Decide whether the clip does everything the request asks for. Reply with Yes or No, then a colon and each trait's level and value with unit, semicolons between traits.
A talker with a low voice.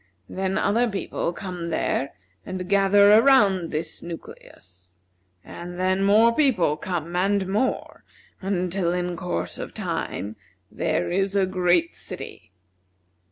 No: medium, 185 Hz